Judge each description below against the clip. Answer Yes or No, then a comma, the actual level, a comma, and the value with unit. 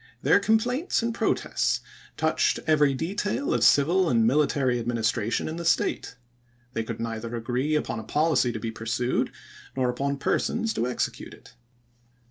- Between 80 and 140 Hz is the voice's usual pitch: Yes, low, 135 Hz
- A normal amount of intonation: No, wide, 5.9 semitones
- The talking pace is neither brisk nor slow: Yes, average, 155 wpm